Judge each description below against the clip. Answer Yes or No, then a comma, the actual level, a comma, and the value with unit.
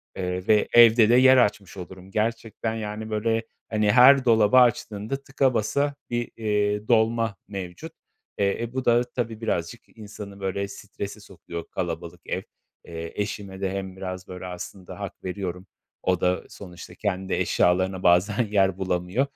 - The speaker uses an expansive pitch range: No, average, 3.6 semitones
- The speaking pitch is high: No, low, 105 Hz